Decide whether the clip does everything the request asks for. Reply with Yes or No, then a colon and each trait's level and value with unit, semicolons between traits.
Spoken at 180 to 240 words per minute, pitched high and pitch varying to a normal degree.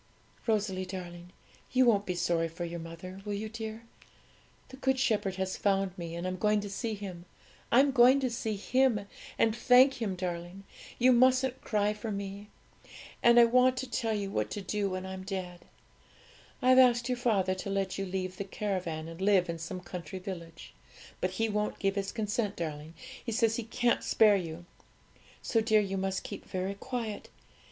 Yes: average, 185 wpm; high, 200 Hz; average, 3.8 semitones